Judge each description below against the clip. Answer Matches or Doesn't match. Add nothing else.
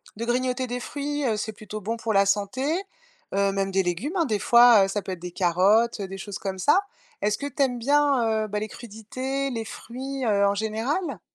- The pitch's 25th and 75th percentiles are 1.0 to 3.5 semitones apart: Doesn't match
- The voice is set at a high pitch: Matches